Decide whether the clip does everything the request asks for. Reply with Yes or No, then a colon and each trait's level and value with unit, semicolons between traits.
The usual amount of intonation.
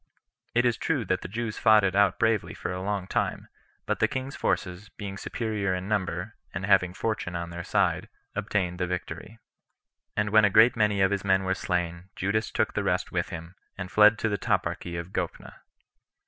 Yes: average, 3.0 semitones